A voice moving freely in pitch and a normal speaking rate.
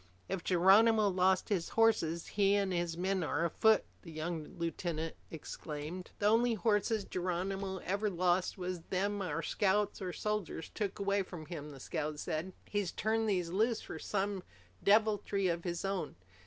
No: average, 3.2 semitones; average, 160 wpm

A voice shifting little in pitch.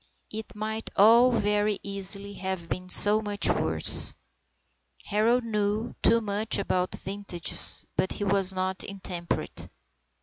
Yes: narrow, 2.2 semitones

